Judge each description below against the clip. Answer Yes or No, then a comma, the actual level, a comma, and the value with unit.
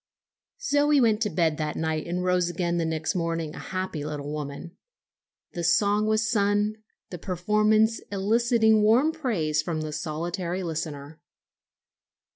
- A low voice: No, medium, 180 Hz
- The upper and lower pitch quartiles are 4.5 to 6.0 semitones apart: Yes, average, 5.1 semitones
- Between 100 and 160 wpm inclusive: Yes, average, 140 wpm